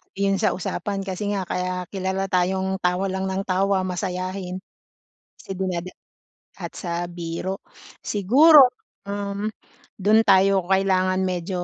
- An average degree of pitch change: No, narrow, 1.3 semitones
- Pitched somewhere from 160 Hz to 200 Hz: Yes, high, 190 Hz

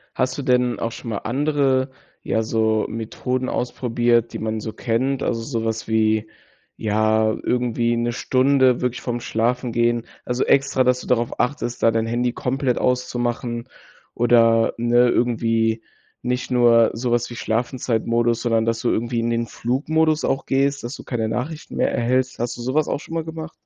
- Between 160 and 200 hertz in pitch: No, low, 120 Hz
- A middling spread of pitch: No, narrow, 1.9 semitones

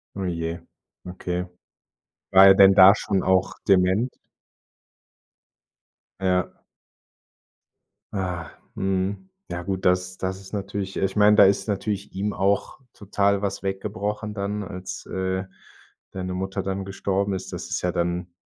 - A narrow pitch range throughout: Yes, narrow, 1.5 semitones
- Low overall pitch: Yes, very low, 95 Hz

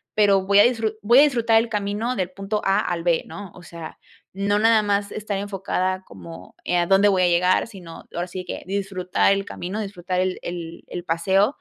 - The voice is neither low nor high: No, high, 195 Hz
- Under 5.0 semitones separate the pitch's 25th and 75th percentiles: Yes, narrow, 2.6 semitones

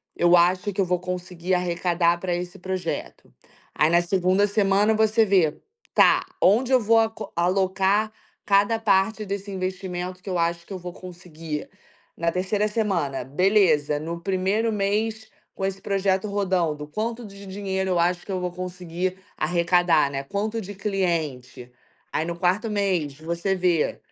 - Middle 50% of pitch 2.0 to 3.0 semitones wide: Yes, average, 2.7 semitones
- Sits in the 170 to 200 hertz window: Yes, medium, 185 Hz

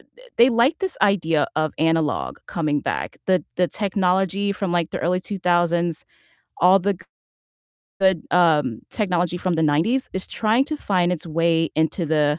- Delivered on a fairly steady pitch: No, average, 3.4 semitones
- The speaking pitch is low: No, medium, 175 Hz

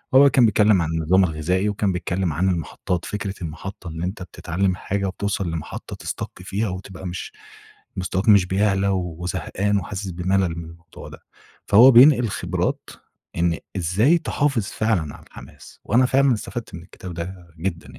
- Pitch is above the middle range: No, very low, 95 Hz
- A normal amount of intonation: Yes, average, 3.1 semitones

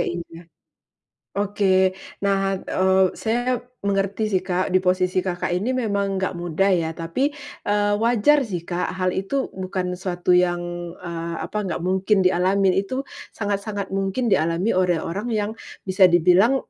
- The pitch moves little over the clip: Yes, narrow, 2.2 semitones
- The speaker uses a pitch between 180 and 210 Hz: Yes, high, 190 Hz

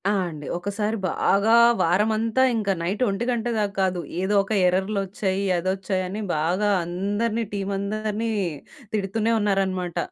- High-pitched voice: Yes, high, 200 Hz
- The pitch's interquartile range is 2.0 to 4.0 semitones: Yes, narrow, 2.4 semitones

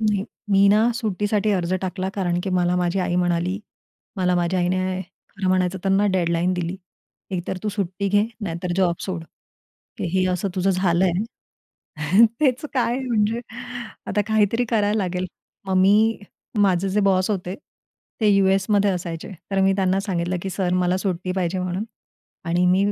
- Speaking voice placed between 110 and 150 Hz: No, high, 190 Hz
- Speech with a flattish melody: Yes, narrow, 2.2 semitones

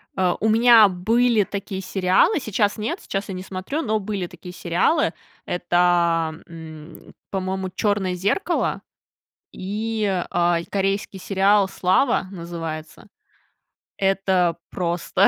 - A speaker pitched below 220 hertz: Yes, high, 190 Hz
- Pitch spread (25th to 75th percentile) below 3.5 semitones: Yes, average, 2.8 semitones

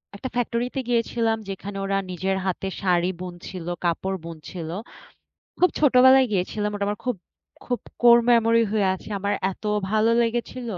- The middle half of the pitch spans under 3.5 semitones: No, average, 4.0 semitones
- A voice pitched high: Yes, high, 210 Hz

